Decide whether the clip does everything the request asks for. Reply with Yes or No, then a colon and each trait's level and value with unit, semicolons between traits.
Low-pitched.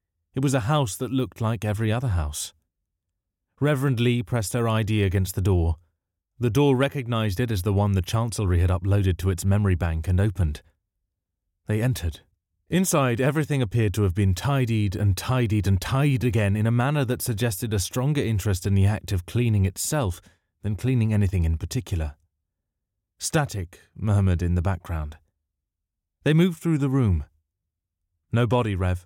Yes: low, 100 Hz